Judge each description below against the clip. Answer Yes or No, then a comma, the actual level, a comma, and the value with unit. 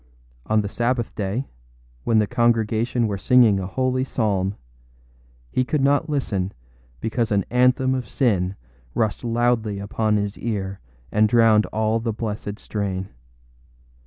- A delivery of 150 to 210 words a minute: No, slow, 135 wpm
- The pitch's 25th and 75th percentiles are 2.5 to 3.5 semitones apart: Yes, average, 3.1 semitones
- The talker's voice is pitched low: Yes, low, 110 Hz